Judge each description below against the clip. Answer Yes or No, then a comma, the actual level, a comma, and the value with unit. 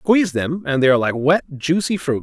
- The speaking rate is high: Yes, fast, 240 wpm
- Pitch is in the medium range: Yes, medium, 155 Hz